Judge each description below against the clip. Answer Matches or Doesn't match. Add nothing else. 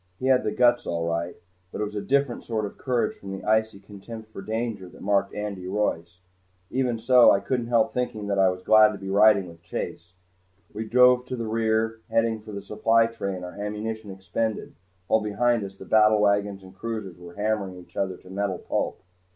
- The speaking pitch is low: Matches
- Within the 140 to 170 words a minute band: Doesn't match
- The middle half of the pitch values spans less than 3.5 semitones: Matches